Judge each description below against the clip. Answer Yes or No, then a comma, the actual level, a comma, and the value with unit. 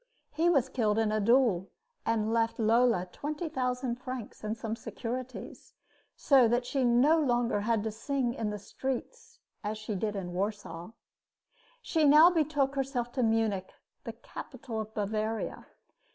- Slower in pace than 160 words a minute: Yes, average, 150 wpm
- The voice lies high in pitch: Yes, high, 235 Hz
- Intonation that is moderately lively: Yes, average, 3.8 semitones